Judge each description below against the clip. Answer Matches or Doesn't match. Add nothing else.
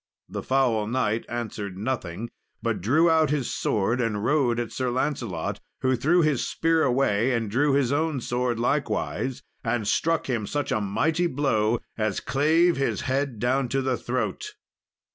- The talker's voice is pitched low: Matches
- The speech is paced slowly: Doesn't match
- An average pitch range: Matches